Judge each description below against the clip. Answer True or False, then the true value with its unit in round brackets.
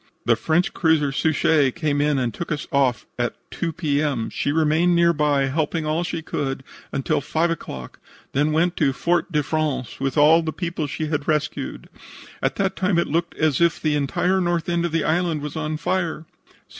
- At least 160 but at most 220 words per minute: True (195 wpm)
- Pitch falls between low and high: True (155 Hz)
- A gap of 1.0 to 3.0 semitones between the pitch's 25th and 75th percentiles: True (2.7 semitones)